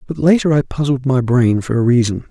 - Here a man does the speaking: Yes, male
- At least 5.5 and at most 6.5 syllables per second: Yes, 5.6 syllables/s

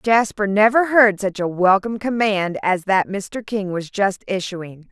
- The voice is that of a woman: Yes, female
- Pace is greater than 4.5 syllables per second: No, 4.2 syllables/s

